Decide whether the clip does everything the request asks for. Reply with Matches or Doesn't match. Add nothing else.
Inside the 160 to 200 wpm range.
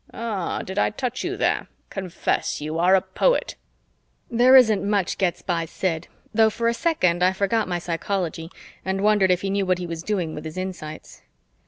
Matches